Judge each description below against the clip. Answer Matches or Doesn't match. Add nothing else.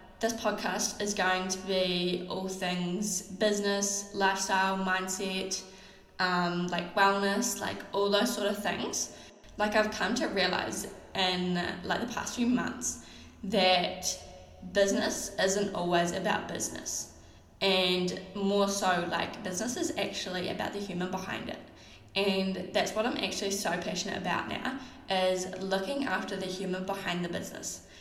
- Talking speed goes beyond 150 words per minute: Doesn't match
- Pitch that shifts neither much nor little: Doesn't match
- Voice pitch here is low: Doesn't match